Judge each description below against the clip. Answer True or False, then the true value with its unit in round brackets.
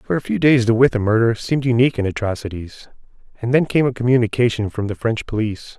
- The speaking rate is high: True (210 wpm)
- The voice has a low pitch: True (115 Hz)